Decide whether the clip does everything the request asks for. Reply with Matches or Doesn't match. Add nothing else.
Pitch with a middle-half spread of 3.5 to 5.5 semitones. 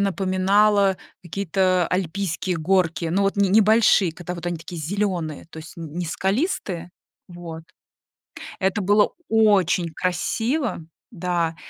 Doesn't match